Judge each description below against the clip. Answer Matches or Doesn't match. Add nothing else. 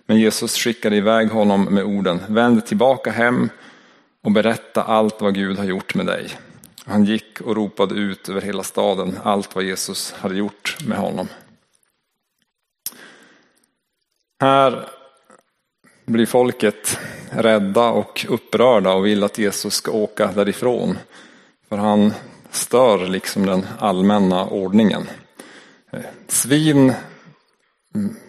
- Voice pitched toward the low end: Matches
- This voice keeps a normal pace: Doesn't match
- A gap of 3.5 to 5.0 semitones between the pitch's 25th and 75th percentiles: Doesn't match